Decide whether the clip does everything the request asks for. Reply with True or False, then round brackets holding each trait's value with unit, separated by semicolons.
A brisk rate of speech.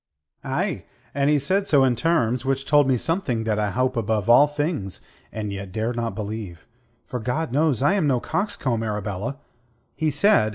False (180 wpm)